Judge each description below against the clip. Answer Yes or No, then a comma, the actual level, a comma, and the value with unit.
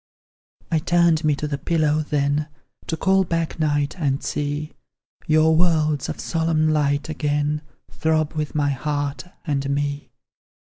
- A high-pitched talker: No, medium, 150 Hz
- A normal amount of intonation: No, narrow, 1.7 semitones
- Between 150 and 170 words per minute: No, average, 140 wpm